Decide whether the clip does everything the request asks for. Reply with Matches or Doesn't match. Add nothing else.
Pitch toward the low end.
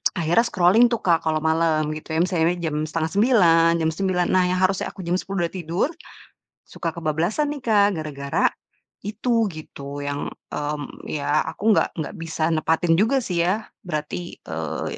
Doesn't match